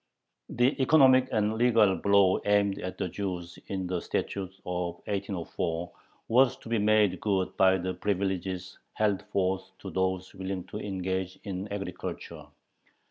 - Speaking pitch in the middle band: No, very low, 95 Hz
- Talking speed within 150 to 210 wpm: No, average, 140 wpm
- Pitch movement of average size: No, narrow, 1.9 semitones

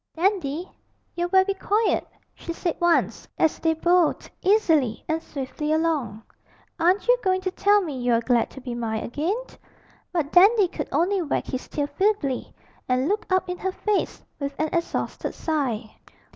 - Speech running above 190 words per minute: No, average, 160 wpm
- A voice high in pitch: Yes, very high, 330 Hz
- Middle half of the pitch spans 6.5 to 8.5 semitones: No, average, 5.3 semitones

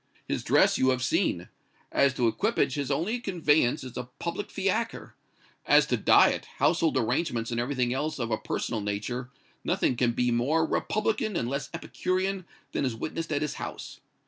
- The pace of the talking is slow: No, average, 170 wpm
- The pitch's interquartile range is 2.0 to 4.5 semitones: No, wide, 5.6 semitones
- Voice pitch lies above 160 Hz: No, medium, 140 Hz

